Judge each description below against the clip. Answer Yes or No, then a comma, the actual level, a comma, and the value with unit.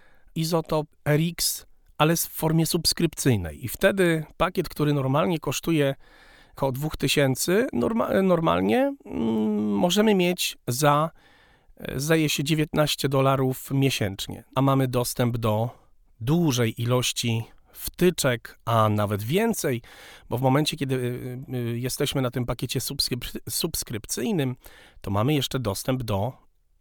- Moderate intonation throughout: Yes, average, 4.6 semitones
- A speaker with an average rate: No, slow, 105 wpm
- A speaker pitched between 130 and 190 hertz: Yes, low, 135 Hz